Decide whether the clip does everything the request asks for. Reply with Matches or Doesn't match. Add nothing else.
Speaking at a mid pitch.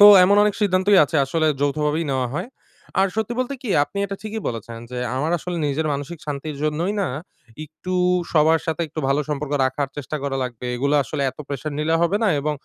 Matches